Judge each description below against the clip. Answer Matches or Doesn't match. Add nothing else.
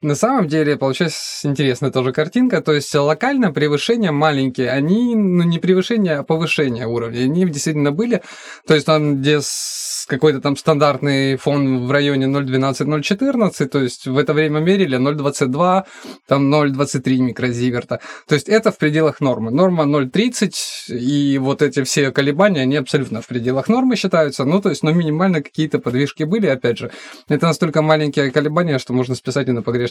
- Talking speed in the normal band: Doesn't match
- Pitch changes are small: Doesn't match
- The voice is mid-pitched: Matches